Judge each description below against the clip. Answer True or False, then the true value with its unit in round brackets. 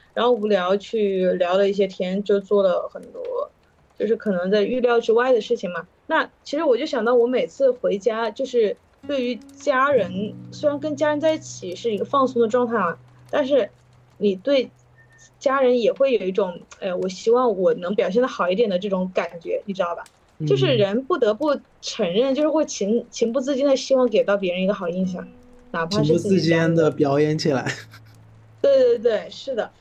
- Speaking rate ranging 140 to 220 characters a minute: False (280 characters per minute)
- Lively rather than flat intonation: True (7.1 semitones)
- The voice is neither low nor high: False (220 Hz)